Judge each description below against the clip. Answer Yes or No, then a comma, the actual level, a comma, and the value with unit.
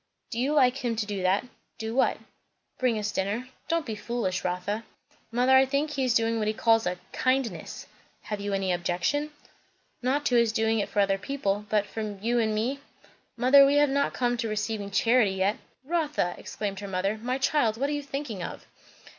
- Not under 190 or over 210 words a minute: Yes, average, 200 wpm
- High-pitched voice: Yes, high, 225 Hz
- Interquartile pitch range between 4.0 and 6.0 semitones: Yes, average, 4.5 semitones